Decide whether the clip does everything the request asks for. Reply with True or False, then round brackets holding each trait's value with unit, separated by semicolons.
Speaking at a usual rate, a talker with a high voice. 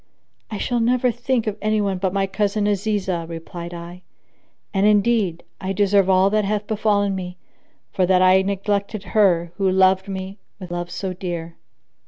True (170 wpm; 195 Hz)